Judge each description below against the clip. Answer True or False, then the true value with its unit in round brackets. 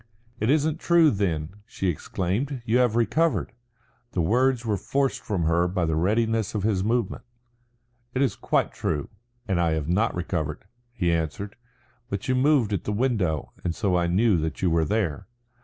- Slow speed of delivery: False (175 wpm)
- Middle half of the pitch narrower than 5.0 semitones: False (5.6 semitones)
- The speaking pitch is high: False (100 Hz)